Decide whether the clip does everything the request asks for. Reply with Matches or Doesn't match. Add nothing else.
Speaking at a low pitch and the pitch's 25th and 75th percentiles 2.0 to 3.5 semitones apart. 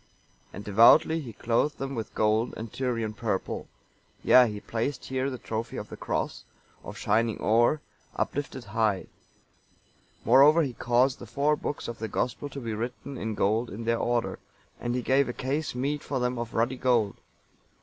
Matches